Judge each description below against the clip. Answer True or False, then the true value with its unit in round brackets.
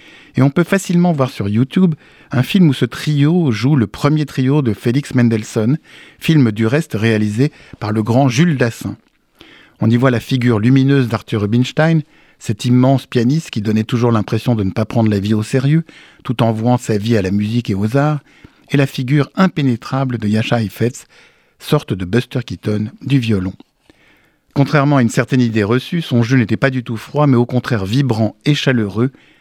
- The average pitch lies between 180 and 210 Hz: False (125 Hz)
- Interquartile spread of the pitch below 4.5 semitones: True (4.0 semitones)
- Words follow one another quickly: False (190 wpm)